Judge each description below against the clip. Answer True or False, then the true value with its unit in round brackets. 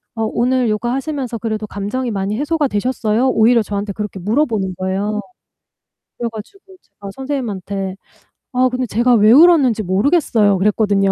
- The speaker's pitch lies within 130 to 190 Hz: False (220 Hz)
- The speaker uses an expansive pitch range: False (4.0 semitones)